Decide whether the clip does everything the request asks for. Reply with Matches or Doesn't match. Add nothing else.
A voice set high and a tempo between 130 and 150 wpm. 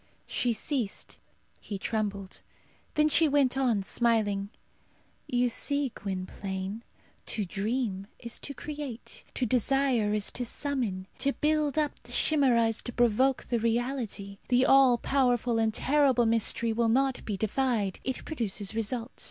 Matches